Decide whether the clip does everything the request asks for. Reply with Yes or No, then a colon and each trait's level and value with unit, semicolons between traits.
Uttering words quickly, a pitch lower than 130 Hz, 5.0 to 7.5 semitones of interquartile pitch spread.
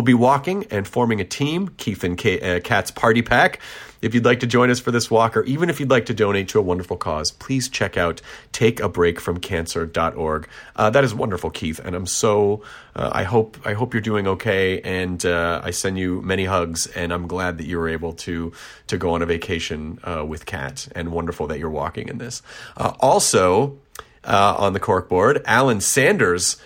Yes: fast, 210 wpm; very low, 95 Hz; wide, 5.6 semitones